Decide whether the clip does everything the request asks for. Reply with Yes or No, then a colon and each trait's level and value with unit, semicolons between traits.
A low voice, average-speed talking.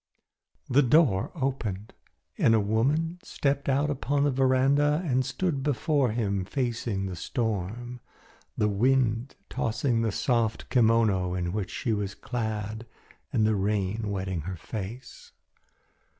No: low, 115 Hz; slow, 130 wpm